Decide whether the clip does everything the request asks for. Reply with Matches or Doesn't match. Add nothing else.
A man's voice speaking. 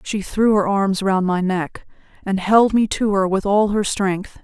Doesn't match